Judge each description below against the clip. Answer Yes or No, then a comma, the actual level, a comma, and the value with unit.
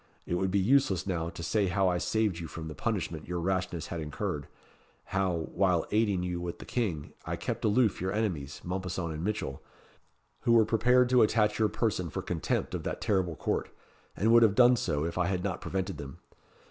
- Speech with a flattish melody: No, average, 4.1 semitones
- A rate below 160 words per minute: No, fast, 205 wpm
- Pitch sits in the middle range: No, very low, 95 Hz